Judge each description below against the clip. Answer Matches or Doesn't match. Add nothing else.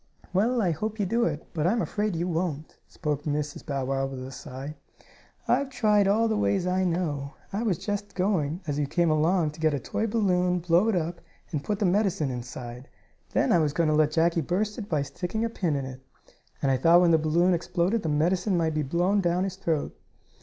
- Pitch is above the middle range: Doesn't match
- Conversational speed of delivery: Doesn't match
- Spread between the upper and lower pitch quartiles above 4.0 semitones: Matches